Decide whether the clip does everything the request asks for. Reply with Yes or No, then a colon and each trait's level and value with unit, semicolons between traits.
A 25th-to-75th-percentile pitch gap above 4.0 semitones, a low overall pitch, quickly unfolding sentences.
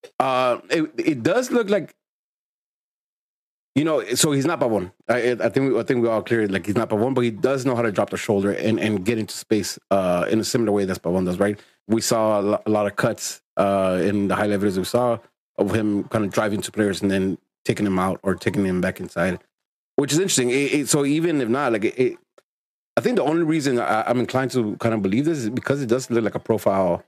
Yes: average, 4.4 semitones; low, 110 Hz; fast, 255 wpm